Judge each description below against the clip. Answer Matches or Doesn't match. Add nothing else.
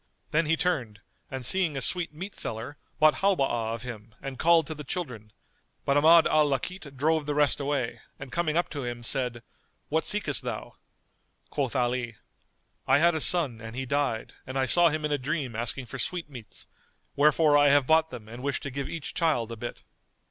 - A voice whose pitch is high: Doesn't match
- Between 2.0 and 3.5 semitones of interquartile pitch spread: Doesn't match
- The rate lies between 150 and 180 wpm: Doesn't match